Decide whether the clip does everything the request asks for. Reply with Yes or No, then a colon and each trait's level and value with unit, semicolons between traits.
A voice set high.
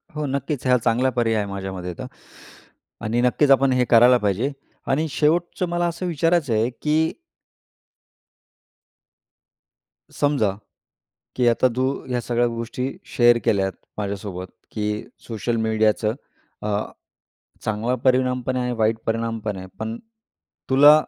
No: low, 120 Hz